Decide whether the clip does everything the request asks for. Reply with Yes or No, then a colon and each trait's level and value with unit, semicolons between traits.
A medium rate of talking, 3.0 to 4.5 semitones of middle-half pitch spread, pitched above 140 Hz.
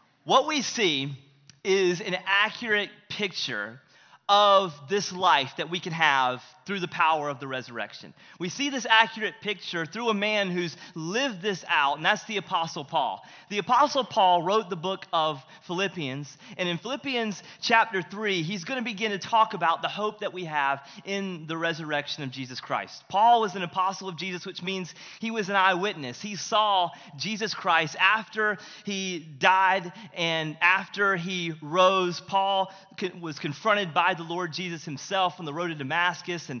Yes: average, 170 wpm; average, 3.9 semitones; medium, 185 Hz